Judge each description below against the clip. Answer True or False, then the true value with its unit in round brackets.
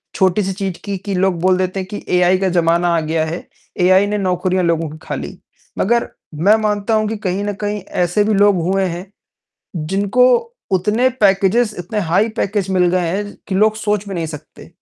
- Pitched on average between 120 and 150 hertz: False (190 Hz)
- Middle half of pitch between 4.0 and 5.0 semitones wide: False (2.6 semitones)